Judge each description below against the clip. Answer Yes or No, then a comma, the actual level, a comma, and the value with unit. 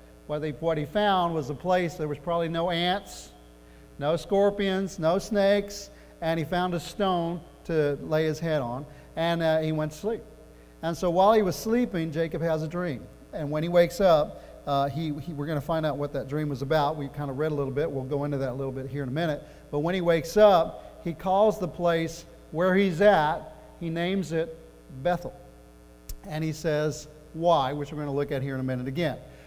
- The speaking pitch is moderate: Yes, medium, 160 Hz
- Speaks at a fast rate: Yes, fast, 225 wpm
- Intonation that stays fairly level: No, average, 3.3 semitones